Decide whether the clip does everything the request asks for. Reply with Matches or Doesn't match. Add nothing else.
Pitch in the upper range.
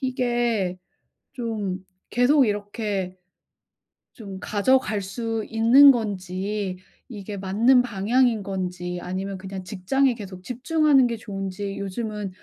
Matches